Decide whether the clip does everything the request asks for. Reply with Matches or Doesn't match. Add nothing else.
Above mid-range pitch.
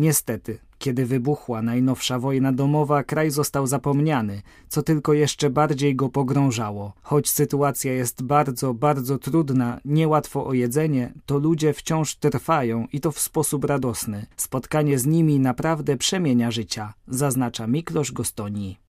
Doesn't match